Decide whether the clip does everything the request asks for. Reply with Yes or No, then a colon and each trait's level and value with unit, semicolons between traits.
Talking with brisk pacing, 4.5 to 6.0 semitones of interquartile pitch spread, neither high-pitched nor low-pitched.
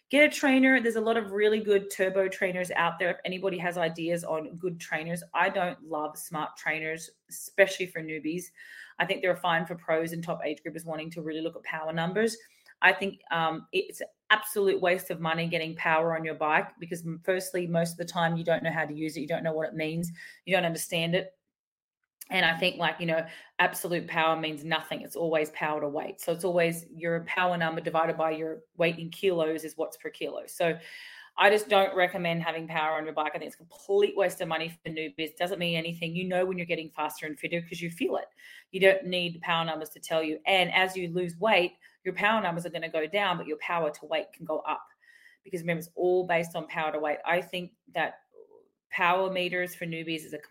No: fast, 235 wpm; narrow, 2.5 semitones; medium, 170 Hz